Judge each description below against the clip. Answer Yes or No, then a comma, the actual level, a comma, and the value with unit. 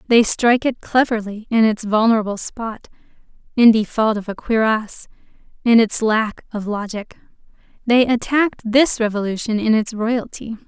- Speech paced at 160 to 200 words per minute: No, average, 140 wpm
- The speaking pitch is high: Yes, high, 225 Hz